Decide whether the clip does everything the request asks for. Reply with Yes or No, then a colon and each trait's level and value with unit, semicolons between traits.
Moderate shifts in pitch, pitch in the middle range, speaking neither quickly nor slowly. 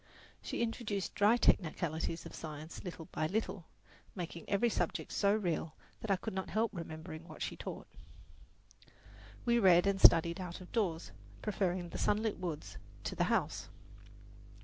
Yes: average, 3.9 semitones; medium, 180 Hz; average, 150 wpm